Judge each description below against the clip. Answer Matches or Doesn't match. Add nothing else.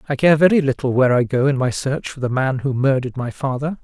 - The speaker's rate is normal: Doesn't match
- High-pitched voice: Doesn't match